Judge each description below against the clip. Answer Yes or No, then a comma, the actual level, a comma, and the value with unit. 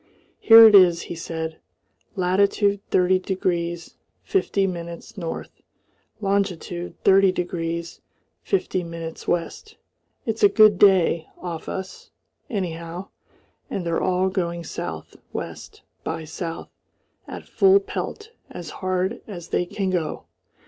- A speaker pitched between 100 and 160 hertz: No, medium, 180 Hz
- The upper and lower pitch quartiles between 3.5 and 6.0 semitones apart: No, average, 2.8 semitones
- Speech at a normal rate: No, slow, 120 wpm